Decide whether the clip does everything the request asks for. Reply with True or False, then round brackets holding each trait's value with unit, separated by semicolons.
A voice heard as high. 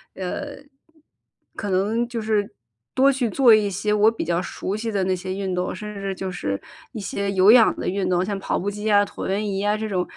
True (200 Hz)